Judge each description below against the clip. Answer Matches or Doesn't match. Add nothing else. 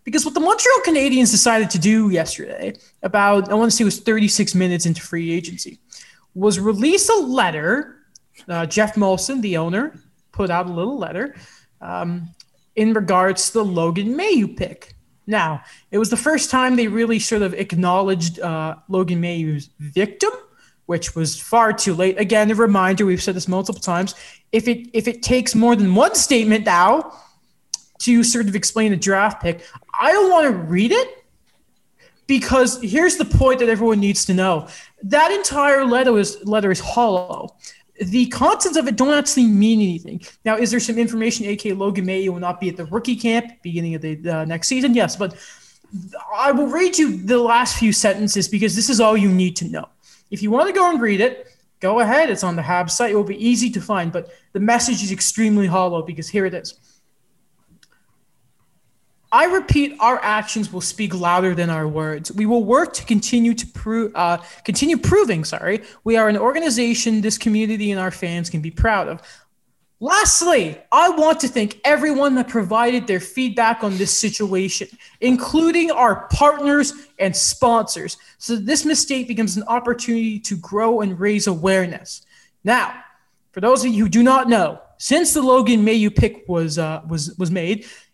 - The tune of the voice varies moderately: Matches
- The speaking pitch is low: Doesn't match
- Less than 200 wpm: Matches